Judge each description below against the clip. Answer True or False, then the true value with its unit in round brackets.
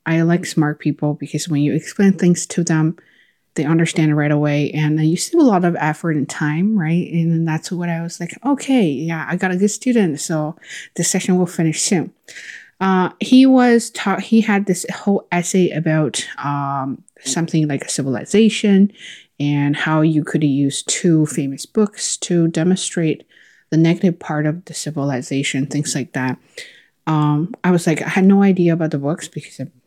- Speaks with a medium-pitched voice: True (165 Hz)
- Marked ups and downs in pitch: False (3.7 semitones)